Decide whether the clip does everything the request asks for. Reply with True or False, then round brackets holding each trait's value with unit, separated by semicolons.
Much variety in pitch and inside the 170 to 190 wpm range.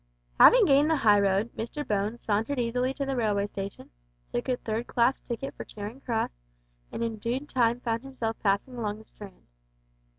False (3.6 semitones; 185 wpm)